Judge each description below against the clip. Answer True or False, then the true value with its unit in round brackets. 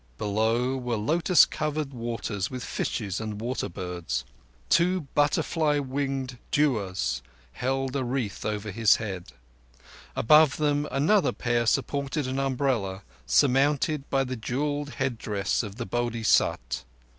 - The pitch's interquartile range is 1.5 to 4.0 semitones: False (4.8 semitones)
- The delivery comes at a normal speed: False (120 wpm)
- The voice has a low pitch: True (125 Hz)